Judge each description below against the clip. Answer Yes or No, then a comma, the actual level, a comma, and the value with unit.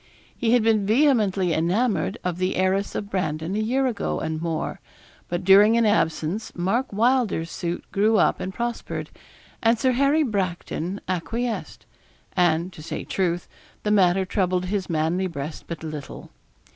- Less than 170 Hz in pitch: No, high, 190 Hz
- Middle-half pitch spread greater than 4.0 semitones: Yes, average, 4.5 semitones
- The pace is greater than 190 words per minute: No, average, 155 wpm